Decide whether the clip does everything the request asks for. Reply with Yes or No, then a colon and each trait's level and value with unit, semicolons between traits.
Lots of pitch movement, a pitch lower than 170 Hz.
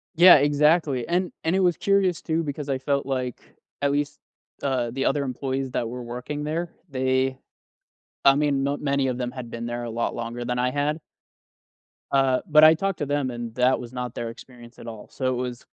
No: average, 3.1 semitones; low, 135 Hz